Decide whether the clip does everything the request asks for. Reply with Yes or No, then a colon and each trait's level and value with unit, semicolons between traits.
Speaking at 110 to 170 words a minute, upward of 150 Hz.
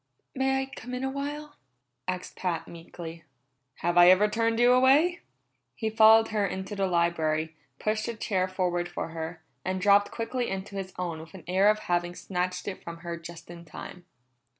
No: average, 185 wpm; medium, 185 Hz